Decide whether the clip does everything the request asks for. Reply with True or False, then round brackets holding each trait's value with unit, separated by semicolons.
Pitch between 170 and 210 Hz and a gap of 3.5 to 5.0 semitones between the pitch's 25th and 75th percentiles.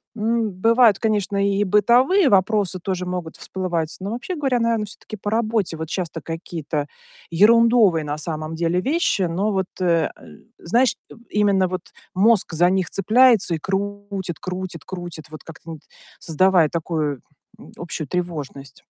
True (190 Hz; 4.4 semitones)